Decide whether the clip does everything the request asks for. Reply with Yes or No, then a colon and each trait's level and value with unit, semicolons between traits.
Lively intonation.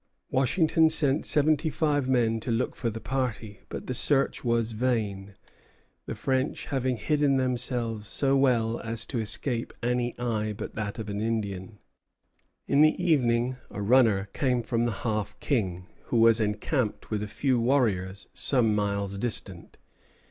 No: average, 3.6 semitones